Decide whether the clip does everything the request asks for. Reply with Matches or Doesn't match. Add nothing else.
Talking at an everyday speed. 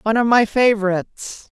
Matches